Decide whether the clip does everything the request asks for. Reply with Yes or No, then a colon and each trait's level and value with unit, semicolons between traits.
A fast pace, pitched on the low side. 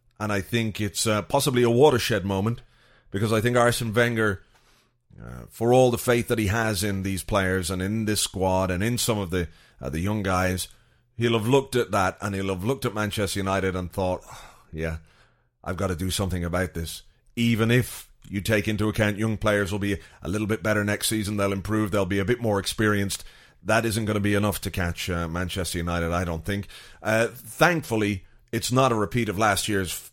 Yes: fast, 215 wpm; low, 105 Hz